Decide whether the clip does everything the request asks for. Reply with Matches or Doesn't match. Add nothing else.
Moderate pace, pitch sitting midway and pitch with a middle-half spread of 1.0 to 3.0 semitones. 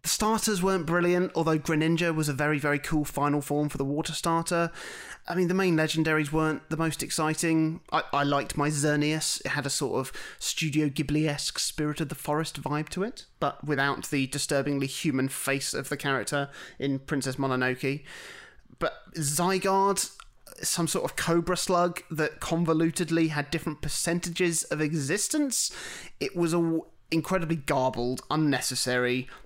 Matches